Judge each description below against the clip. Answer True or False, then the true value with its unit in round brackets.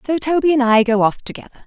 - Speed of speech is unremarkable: False (255 wpm)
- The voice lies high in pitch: True (260 Hz)